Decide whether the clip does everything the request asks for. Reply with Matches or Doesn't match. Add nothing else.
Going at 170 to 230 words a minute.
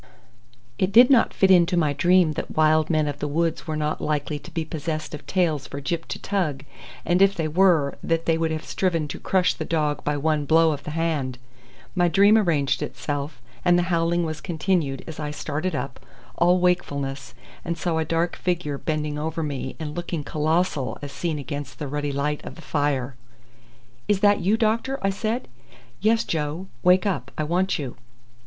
Matches